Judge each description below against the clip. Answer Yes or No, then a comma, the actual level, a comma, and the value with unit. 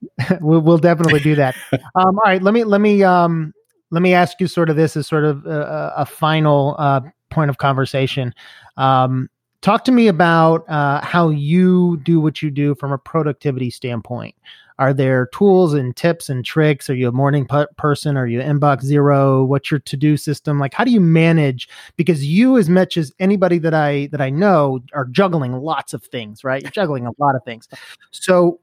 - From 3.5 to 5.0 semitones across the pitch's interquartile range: Yes, average, 3.8 semitones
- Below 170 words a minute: No, average, 200 wpm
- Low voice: No, medium, 150 Hz